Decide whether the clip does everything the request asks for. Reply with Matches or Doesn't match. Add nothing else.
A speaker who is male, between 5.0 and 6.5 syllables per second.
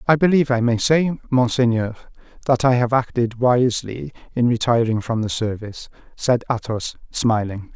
Matches